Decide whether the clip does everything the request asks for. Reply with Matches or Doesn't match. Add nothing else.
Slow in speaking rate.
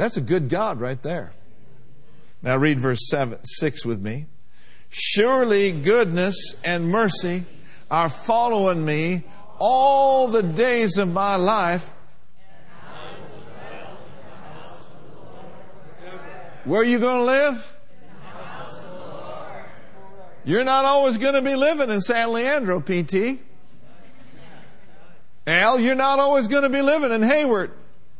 Matches